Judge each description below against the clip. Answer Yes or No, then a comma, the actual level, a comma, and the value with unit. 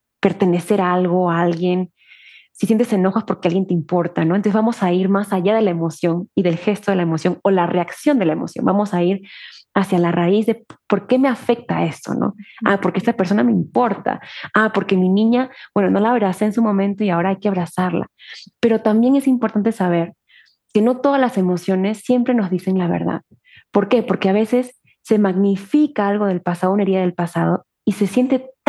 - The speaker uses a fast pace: Yes, fast, 215 wpm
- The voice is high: Yes, high, 200 Hz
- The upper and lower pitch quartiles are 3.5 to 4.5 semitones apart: Yes, average, 3.8 semitones